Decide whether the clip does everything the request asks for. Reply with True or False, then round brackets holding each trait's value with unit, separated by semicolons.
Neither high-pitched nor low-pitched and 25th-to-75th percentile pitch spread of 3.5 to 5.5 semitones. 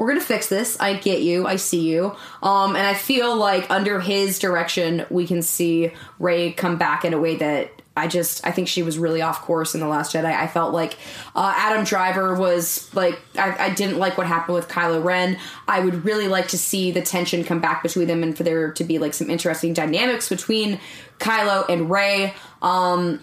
False (175 Hz; 2.7 semitones)